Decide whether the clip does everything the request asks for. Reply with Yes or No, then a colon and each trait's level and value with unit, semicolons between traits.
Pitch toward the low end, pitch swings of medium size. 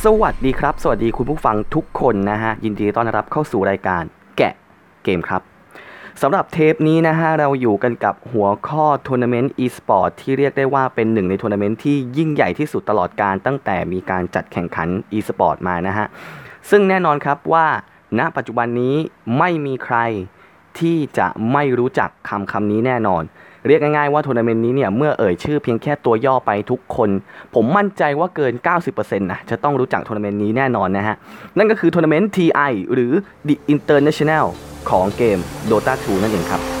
No: low, 125 Hz; wide, 6.0 semitones